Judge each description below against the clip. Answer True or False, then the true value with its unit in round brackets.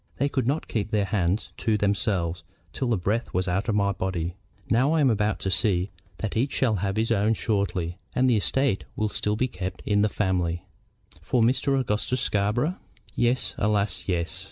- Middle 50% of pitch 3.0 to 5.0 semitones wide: True (4.0 semitones)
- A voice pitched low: True (105 Hz)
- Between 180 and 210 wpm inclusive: True (190 wpm)